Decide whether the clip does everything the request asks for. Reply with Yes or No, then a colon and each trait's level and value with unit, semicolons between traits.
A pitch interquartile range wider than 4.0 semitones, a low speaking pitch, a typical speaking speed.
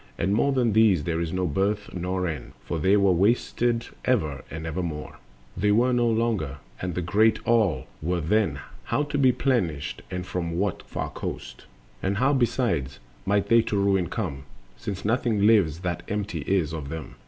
Yes: average, 5.2 semitones; very low, 95 Hz; average, 180 wpm